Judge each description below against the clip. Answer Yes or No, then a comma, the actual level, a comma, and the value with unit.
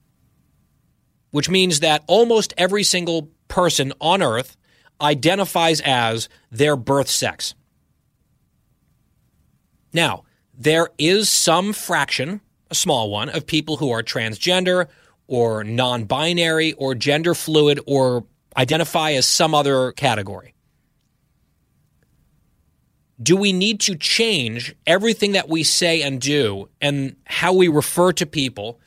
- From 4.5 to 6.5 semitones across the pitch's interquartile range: Yes, average, 5.2 semitones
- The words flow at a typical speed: No, slow, 115 wpm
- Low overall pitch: No, medium, 155 Hz